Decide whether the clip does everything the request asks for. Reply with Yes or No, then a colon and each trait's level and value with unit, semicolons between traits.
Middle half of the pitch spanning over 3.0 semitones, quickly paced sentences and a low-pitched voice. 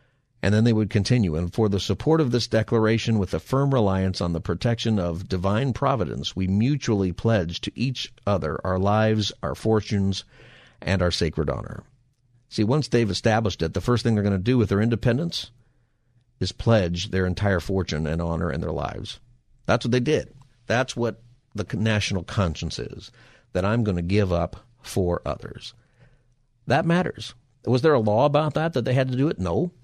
No: average, 4.5 semitones; average, 190 wpm; low, 110 Hz